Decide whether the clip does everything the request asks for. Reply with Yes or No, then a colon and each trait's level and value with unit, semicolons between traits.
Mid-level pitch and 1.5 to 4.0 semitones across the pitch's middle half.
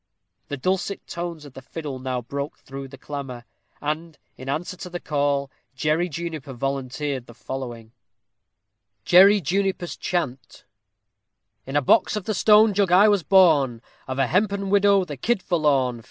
No: medium, 150 Hz; wide, 5.5 semitones